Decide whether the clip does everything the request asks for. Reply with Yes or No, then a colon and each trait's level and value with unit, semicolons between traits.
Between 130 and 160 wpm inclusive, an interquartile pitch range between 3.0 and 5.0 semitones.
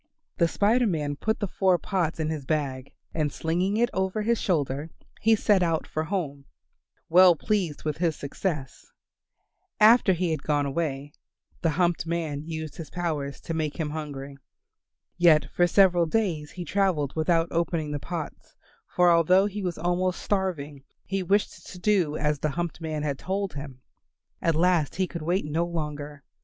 No: average, 170 wpm; average, 3.6 semitones